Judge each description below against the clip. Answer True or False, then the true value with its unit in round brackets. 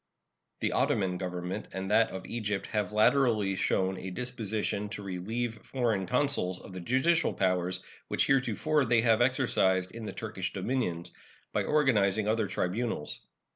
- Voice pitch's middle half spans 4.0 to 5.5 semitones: True (4.3 semitones)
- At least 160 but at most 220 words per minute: False (145 wpm)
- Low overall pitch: True (105 Hz)